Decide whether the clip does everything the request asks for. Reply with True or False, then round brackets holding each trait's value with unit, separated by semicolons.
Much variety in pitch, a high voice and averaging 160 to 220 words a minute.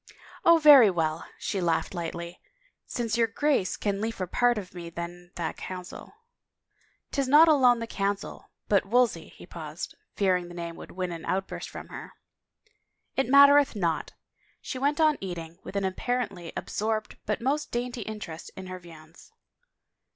True (6.0 semitones; 200 Hz; 180 wpm)